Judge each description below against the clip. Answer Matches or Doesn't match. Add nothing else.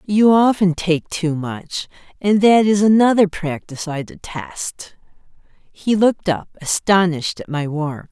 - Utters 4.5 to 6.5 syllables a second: Doesn't match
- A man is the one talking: Doesn't match